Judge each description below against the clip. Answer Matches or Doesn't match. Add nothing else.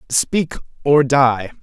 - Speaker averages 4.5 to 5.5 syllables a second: Doesn't match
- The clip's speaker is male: Matches